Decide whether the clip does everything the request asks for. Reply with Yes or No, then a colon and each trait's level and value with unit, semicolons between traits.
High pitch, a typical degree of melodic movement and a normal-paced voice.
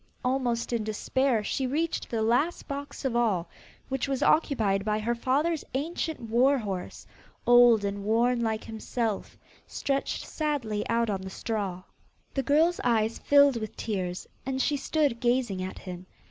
Yes: high, 235 Hz; average, 4.3 semitones; average, 155 wpm